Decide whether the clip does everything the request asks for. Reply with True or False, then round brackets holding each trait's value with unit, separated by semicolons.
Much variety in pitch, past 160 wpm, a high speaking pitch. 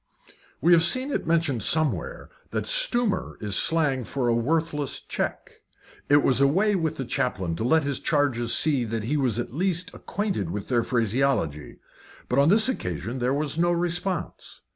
False (5.9 semitones; 175 wpm; 145 Hz)